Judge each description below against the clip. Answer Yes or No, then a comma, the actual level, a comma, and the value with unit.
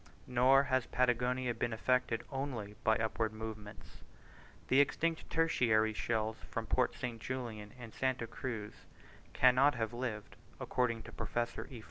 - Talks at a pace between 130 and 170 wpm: Yes, slow, 135 wpm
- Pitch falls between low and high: No, low, 120 Hz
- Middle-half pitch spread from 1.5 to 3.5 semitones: Yes, narrow, 2.5 semitones